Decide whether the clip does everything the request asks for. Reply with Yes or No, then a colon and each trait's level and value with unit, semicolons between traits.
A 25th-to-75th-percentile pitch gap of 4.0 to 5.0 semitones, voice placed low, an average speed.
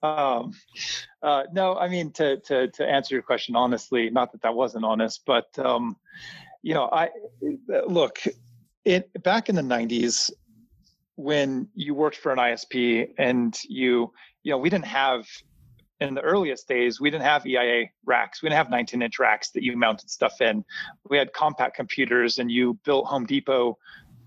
Yes: average, 4.5 semitones; low, 130 Hz; average, 175 wpm